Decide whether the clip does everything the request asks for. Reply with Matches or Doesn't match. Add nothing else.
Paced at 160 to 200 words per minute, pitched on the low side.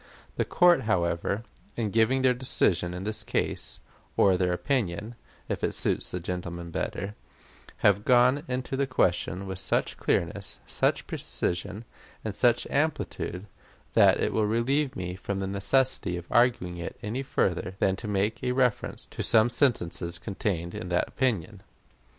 Doesn't match